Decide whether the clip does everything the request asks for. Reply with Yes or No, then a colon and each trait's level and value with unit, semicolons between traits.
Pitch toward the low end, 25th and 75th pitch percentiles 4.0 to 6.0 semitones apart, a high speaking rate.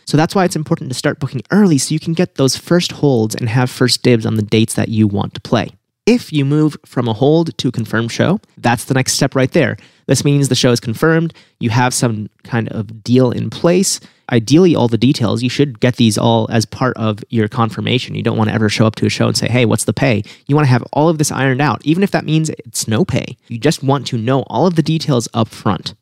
Yes: low, 125 Hz; average, 4.7 semitones; fast, 265 wpm